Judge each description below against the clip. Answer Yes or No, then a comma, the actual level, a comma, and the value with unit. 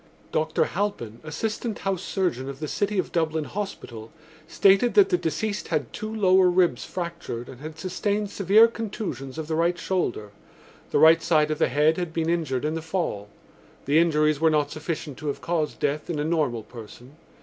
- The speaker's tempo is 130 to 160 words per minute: No, average, 185 wpm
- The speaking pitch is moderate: Yes, medium, 160 Hz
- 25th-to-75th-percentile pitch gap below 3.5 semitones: No, average, 4.0 semitones